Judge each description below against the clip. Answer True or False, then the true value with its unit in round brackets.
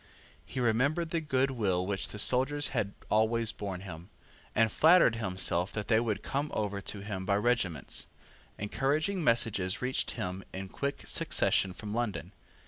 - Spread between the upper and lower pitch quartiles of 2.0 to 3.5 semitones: False (4.9 semitones)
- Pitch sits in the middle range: False (110 Hz)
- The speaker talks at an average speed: True (155 wpm)